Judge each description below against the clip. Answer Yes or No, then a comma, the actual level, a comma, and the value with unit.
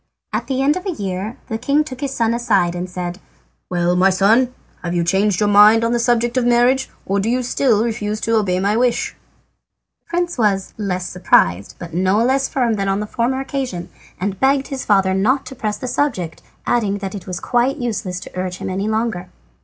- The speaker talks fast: Yes, fast, 215 wpm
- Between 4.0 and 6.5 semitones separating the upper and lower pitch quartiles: Yes, average, 4.7 semitones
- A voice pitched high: Yes, high, 215 Hz